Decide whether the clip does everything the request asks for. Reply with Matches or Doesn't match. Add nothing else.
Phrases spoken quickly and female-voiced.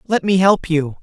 Doesn't match